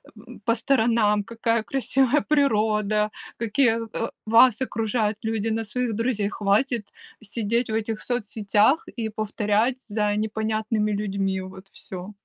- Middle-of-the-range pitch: No, high, 220 Hz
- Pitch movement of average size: No, narrow, 1.8 semitones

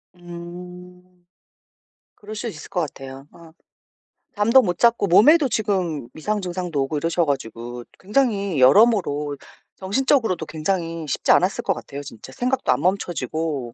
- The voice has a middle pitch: Yes, medium, 175 Hz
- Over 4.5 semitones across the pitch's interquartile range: Yes, average, 5.3 semitones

